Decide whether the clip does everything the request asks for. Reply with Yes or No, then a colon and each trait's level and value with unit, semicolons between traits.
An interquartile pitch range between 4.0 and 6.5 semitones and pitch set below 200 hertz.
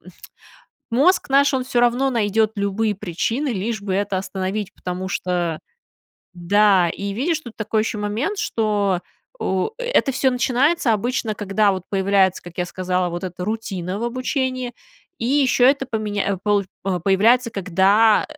No: average, 4.4 semitones; high, 210 Hz